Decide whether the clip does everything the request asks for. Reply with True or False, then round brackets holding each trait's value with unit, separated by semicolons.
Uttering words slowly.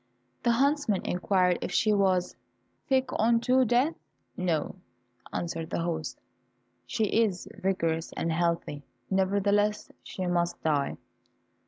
True (115 wpm)